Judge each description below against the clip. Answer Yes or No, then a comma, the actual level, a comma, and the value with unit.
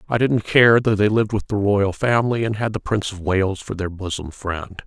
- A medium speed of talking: No, fast, 245 wpm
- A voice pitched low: Yes, low, 105 Hz